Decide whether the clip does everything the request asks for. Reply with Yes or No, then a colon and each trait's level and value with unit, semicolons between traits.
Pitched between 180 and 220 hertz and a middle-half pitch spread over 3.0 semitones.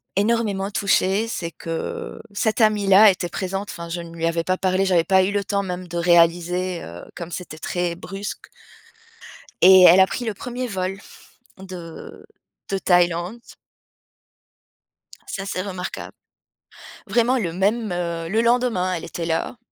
No: medium, 185 Hz; average, 2.7 semitones